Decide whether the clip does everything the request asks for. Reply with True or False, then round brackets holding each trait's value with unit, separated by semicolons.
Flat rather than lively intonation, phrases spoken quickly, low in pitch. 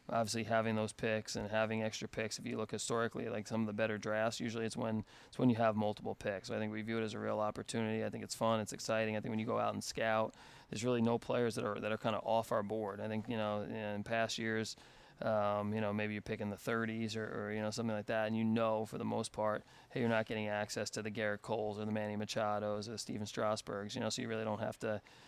True (1.0 semitones; 280 wpm; 110 Hz)